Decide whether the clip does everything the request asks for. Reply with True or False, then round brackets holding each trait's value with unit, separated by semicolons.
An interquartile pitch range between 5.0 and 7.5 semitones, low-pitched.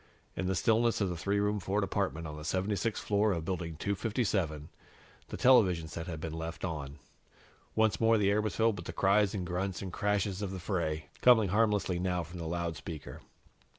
False (3.8 semitones; 95 Hz)